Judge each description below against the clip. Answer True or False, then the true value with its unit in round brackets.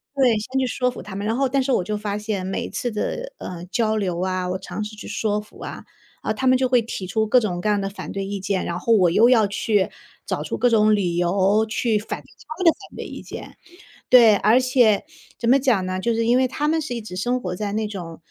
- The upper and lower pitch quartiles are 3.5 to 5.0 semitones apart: True (4.0 semitones)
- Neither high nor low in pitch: False (215 Hz)